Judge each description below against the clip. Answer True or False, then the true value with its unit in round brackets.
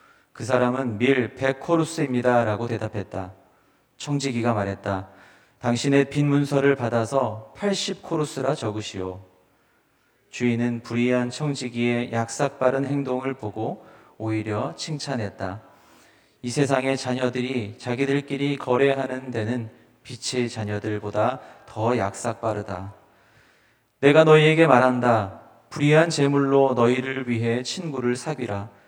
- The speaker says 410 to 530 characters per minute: False (260 characters per minute)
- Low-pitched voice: True (125 Hz)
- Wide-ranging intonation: False (3.8 semitones)